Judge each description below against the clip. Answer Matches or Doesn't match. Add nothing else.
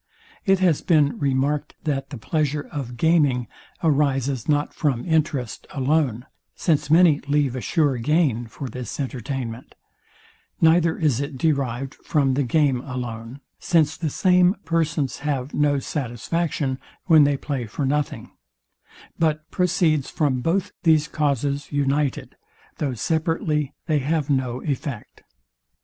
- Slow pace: Matches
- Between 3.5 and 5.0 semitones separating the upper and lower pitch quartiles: Doesn't match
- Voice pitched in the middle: Matches